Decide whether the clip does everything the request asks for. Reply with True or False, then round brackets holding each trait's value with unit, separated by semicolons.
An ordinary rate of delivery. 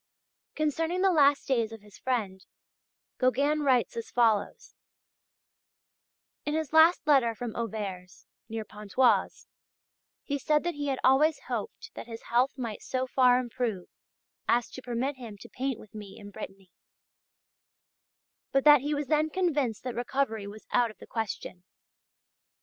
True (150 wpm)